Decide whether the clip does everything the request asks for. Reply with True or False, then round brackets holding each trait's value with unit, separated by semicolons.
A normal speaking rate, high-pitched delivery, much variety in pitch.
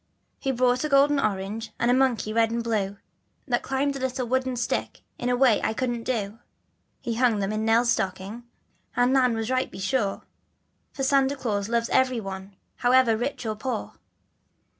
False (180 wpm; 240 Hz; 3.0 semitones)